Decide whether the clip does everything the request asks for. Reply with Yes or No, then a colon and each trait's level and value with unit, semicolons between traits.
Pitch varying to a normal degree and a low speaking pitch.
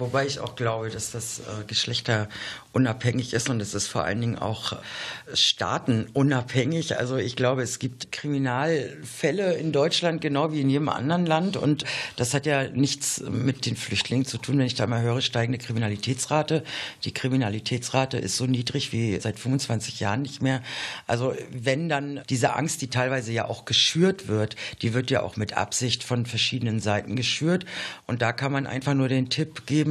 Yes: average, 3.1 semitones; low, 125 Hz